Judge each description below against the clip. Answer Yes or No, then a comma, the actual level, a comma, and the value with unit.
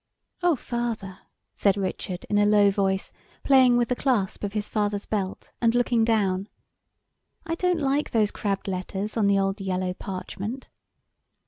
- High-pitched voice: Yes, high, 205 Hz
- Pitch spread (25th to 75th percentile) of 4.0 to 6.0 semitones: No, average, 3.6 semitones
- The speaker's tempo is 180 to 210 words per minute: No, average, 155 wpm